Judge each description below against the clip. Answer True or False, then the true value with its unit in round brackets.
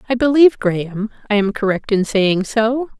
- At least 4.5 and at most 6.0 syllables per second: True (5.1 syllables/s)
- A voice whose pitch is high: True (225 Hz)